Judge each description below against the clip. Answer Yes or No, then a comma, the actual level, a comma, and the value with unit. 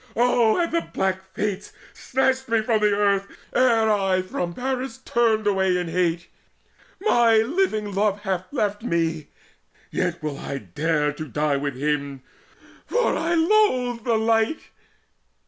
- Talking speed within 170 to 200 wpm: No, average, 145 wpm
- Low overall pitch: No, high, 210 Hz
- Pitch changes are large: Yes, wide, 6.0 semitones